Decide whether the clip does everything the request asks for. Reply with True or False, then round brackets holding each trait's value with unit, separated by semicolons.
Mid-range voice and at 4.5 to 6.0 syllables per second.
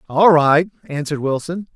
True (160 Hz; 5.2 syllables/s)